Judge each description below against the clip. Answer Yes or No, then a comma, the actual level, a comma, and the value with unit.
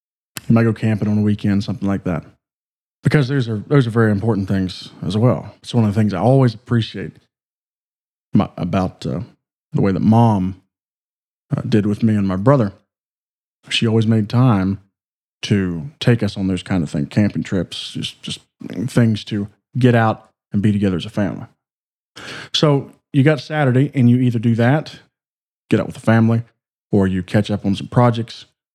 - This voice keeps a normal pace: Yes, average, 185 wpm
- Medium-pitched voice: No, low, 110 Hz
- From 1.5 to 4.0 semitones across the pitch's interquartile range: Yes, average, 3.5 semitones